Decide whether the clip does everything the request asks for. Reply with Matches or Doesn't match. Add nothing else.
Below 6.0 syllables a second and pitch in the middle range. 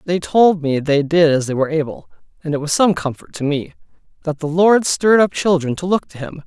Matches